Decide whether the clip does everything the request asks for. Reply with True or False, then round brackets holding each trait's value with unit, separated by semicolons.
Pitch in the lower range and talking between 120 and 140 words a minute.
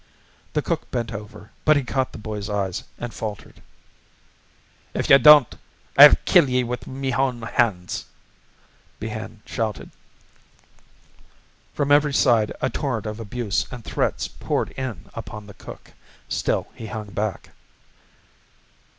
True (115 Hz; 135 wpm)